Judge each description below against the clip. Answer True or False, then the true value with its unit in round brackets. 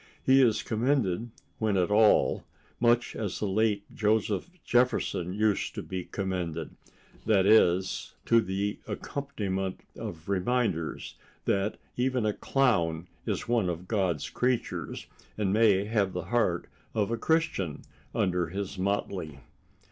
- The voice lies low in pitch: True (100 Hz)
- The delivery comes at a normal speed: False (125 wpm)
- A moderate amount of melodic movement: True (3.8 semitones)